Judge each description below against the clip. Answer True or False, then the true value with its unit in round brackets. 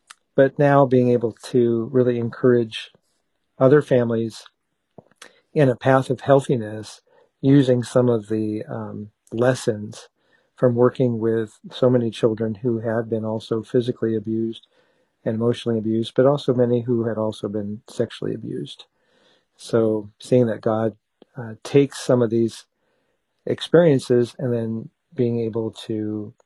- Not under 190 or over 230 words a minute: False (135 wpm)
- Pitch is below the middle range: True (120 Hz)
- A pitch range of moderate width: False (2.2 semitones)